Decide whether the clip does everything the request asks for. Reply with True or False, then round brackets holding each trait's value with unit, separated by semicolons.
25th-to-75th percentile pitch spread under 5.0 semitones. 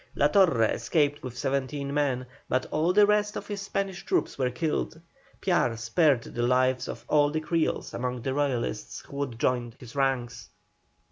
True (4.5 semitones)